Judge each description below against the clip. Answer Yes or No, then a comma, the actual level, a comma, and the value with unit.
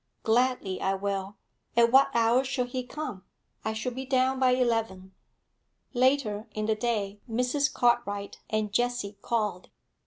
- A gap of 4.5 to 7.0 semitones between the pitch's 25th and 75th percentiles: No, average, 3.5 semitones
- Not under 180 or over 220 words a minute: No, average, 145 wpm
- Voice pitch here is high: Yes, high, 235 Hz